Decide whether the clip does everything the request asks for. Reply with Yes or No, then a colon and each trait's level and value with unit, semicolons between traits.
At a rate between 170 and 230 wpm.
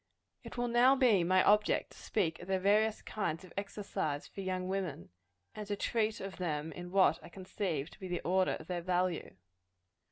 Yes: average, 195 wpm